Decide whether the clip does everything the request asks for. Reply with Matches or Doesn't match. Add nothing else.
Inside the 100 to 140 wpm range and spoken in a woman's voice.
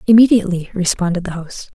Matches